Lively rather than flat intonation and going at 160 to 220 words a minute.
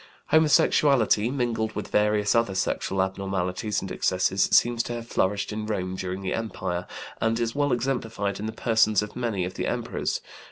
No: average, 3.4 semitones; average, 170 wpm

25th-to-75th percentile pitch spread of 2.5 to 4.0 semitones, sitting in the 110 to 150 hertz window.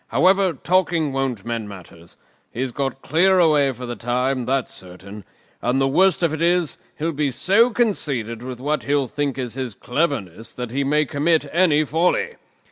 No: average, 5.1 semitones; medium, 140 Hz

